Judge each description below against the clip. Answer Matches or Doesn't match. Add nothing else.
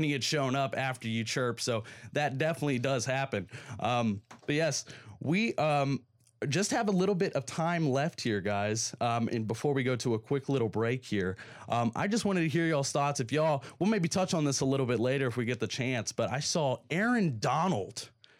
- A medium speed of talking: Doesn't match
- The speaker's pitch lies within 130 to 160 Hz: Matches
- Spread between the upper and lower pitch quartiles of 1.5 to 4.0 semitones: Doesn't match